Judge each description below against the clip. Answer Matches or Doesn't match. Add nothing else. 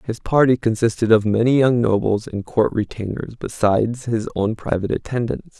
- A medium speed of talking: Matches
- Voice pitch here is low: Matches